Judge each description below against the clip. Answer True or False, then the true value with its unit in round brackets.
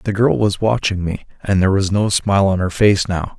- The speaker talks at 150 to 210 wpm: False (250 wpm)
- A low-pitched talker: True (100 Hz)